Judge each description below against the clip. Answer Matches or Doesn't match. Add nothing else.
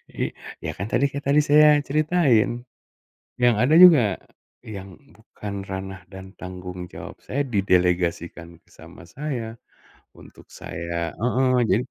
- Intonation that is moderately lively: Doesn't match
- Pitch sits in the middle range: Doesn't match